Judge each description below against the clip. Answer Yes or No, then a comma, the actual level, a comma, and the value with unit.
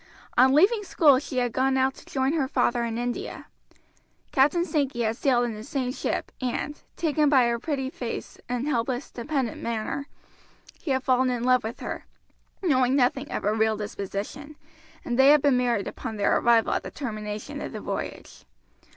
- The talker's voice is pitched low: No, very high, 255 Hz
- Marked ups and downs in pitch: No, average, 3.0 semitones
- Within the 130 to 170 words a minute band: No, average, 185 wpm